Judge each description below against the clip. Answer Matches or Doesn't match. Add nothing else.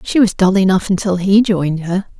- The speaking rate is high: Matches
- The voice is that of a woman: Matches